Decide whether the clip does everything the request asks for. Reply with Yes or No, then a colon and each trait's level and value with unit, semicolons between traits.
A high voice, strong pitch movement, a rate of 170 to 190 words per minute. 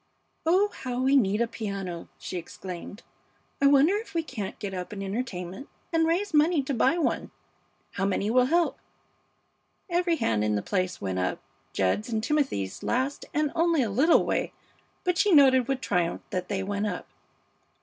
Yes: high, 240 Hz; wide, 7.9 semitones; average, 175 wpm